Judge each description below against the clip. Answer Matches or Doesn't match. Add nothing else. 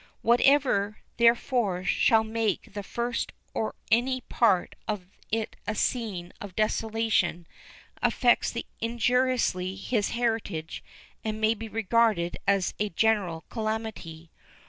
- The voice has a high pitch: Matches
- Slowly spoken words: Matches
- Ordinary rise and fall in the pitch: Matches